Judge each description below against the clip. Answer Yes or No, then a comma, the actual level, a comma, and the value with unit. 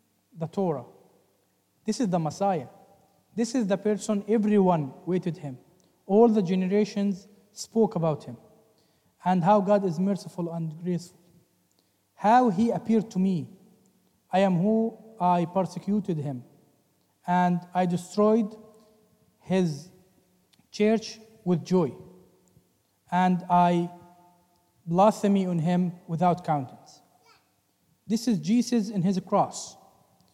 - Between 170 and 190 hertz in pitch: Yes, medium, 185 Hz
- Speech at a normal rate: No, slow, 115 wpm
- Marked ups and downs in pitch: No, average, 3.3 semitones